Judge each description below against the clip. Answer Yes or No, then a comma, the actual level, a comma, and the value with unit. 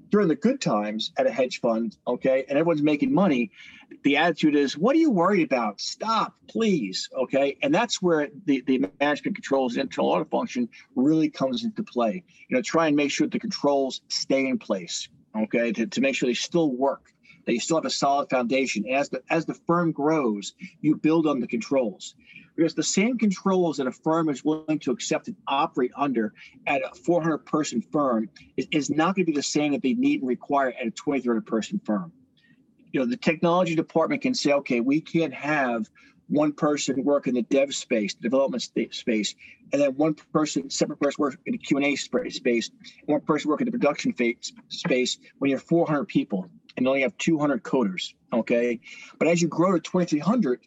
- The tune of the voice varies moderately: No, wide, 6.2 semitones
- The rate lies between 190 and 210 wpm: Yes, average, 200 wpm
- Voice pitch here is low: No, medium, 155 Hz